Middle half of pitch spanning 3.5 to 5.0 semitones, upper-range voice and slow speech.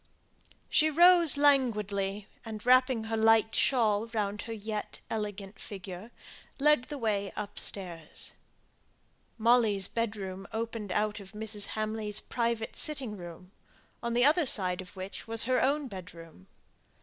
No: average, 3.1 semitones; high, 215 Hz; slow, 130 wpm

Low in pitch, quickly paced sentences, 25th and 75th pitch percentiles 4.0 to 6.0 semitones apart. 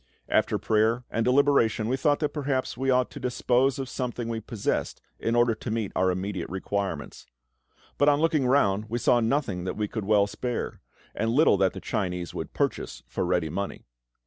No: low, 115 Hz; average, 190 wpm; average, 4.6 semitones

